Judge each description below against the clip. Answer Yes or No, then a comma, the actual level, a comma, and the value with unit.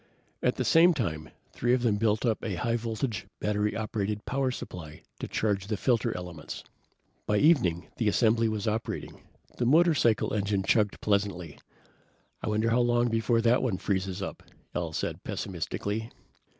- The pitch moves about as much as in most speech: Yes, average, 3.3 semitones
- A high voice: No, low, 110 Hz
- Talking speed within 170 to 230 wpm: No, average, 160 wpm